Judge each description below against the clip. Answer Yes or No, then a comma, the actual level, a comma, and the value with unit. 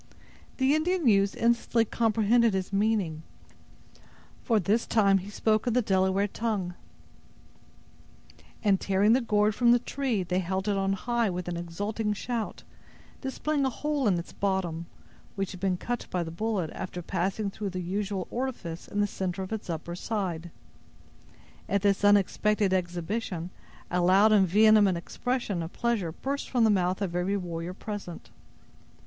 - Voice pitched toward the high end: Yes, high, 200 Hz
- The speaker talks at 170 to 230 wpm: No, average, 155 wpm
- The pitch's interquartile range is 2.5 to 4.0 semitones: Yes, average, 3.6 semitones